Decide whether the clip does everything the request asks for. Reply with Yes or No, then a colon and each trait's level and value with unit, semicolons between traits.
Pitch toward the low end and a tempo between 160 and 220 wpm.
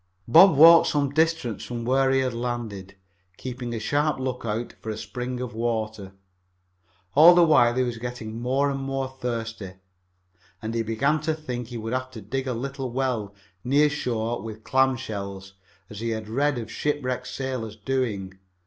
Yes: low, 125 Hz; average, 175 wpm